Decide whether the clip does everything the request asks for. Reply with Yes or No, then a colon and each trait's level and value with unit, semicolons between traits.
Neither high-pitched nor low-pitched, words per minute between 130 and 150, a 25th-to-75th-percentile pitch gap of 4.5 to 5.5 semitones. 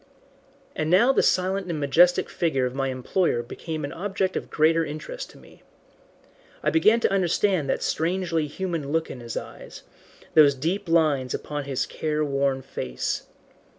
No: medium, 160 Hz; average, 160 wpm; average, 4.8 semitones